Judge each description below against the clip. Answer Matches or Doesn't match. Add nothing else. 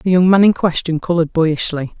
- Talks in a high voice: Doesn't match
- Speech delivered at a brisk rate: Matches